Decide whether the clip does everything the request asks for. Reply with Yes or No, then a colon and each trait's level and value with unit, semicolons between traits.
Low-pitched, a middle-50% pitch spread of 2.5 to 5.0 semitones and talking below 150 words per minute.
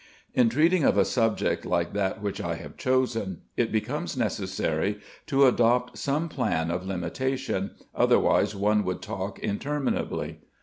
No: low, 110 Hz; wide, 5.4 semitones; average, 140 wpm